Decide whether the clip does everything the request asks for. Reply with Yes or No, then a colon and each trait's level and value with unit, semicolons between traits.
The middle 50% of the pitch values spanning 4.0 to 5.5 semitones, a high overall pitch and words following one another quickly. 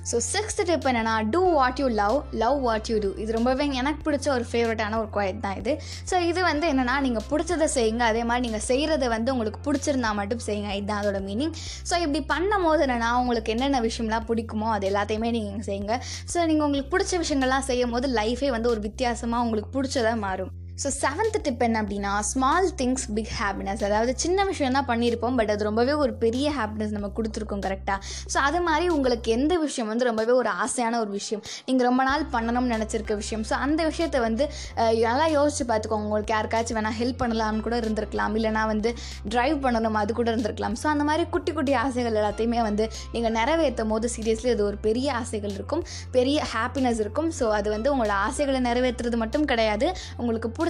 Yes: average, 4.4 semitones; high, 235 Hz; fast, 190 wpm